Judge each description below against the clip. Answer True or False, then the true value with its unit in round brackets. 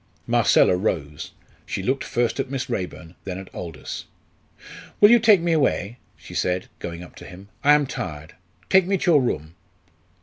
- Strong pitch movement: True (8.9 semitones)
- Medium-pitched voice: False (110 Hz)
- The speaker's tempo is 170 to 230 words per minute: True (175 wpm)